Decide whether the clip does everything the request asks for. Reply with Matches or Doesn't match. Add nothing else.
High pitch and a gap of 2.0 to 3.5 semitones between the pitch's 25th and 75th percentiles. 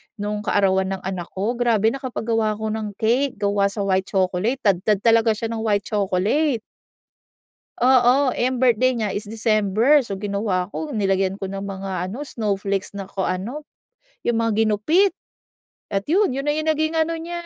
Doesn't match